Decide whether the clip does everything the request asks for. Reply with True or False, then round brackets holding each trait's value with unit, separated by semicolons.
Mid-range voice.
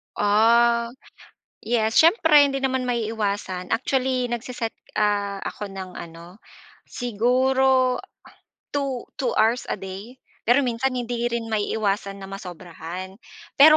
False (230 Hz)